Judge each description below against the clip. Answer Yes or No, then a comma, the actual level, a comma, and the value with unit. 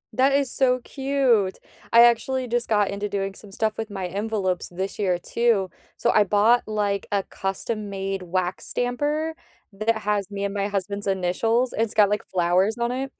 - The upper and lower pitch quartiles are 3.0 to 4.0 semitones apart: Yes, average, 3.4 semitones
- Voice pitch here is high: Yes, high, 210 Hz